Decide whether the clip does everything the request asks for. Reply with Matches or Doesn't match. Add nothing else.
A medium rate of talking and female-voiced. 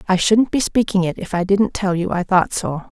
Doesn't match